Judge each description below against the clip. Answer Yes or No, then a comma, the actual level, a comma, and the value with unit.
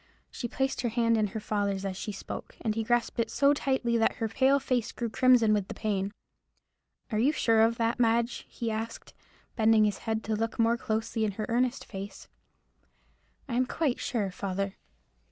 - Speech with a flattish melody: Yes, narrow, 2.1 semitones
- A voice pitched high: Yes, high, 225 Hz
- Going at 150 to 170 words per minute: No, average, 190 wpm